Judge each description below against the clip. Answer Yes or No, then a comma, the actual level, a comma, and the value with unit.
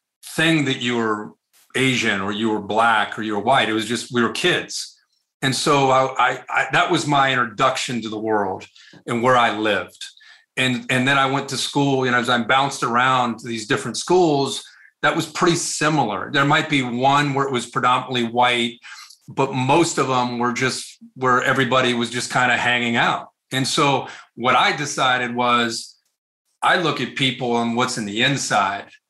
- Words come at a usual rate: Yes, average, 195 wpm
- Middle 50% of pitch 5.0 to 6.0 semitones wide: No, narrow, 2.6 semitones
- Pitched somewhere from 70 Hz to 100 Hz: No, low, 125 Hz